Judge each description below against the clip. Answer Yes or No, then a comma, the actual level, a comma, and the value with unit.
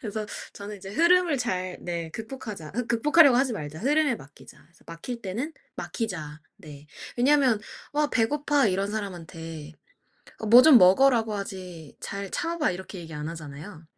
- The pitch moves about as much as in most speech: No, wide, 7.3 semitones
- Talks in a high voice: Yes, high, 205 Hz